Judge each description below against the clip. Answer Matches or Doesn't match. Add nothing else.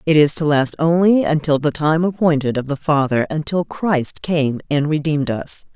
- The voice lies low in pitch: Doesn't match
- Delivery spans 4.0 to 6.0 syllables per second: Matches